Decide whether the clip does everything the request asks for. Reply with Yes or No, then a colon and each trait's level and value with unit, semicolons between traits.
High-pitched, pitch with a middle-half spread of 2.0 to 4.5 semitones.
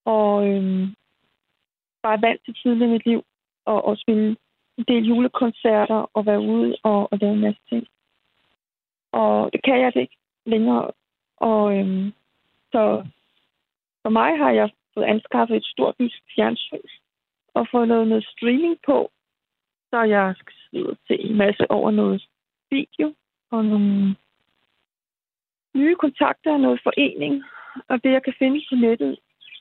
Yes: high, 225 Hz; average, 3.4 semitones